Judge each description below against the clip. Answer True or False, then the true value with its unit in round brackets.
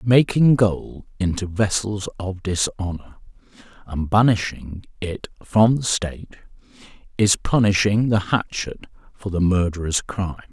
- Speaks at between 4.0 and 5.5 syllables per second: True (4.2 syllables/s)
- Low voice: True (100 Hz)